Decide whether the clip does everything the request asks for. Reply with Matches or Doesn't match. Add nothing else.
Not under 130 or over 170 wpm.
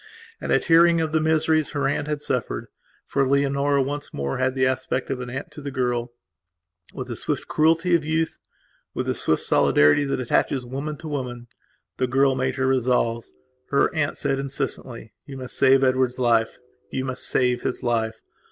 Doesn't match